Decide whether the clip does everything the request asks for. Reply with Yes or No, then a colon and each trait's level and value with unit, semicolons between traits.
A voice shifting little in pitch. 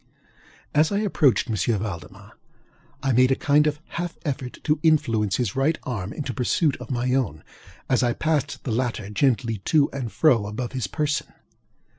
No: average, 5.0 semitones